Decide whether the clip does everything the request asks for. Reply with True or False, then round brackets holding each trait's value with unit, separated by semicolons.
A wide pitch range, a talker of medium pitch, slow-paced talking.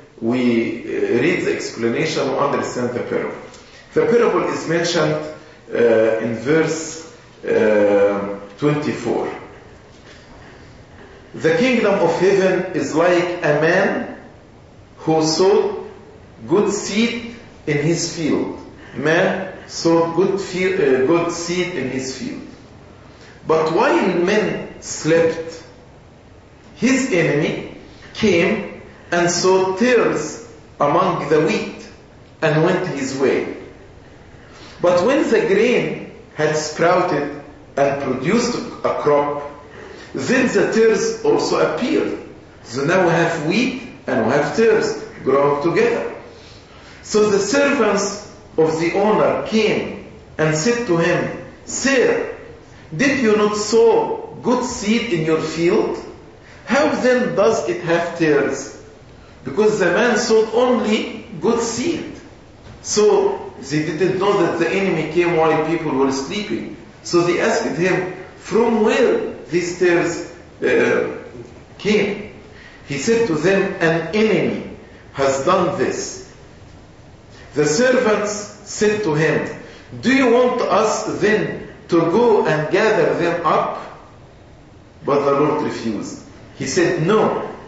True (7.0 semitones; 180 Hz; 120 wpm)